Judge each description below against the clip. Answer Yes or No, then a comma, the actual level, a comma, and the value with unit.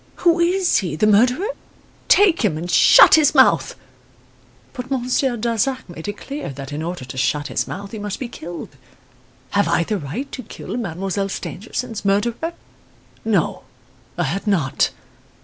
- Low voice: No, high, 210 Hz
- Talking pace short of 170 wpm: Yes, average, 160 wpm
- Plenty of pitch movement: Yes, wide, 6.6 semitones